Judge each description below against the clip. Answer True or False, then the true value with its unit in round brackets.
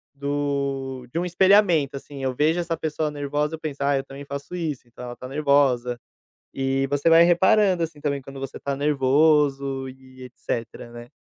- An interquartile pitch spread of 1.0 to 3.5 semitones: True (2.7 semitones)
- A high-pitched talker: False (140 Hz)